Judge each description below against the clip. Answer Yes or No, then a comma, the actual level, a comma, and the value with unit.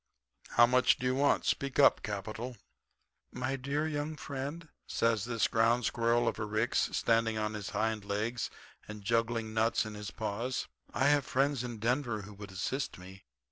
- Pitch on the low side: Yes, low, 115 Hz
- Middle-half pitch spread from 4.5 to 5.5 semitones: No, average, 3.3 semitones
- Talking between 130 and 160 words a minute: No, average, 175 wpm